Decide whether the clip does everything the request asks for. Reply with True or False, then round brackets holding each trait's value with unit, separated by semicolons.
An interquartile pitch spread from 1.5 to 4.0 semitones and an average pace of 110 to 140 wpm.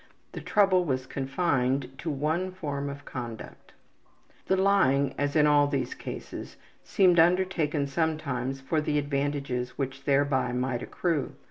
True (3.4 semitones; 135 wpm)